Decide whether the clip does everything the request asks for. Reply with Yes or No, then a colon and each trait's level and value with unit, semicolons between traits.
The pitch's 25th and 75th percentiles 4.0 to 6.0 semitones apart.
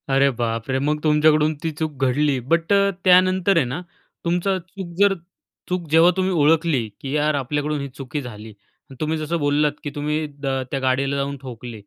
No: average, 3.6 semitones